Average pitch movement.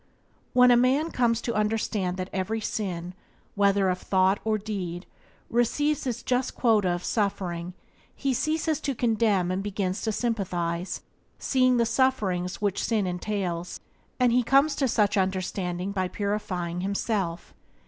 Yes: average, 4.5 semitones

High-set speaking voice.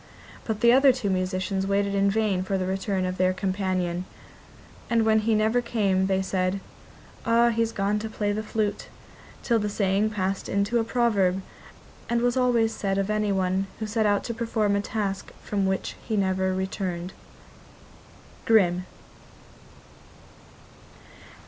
Yes: high, 200 Hz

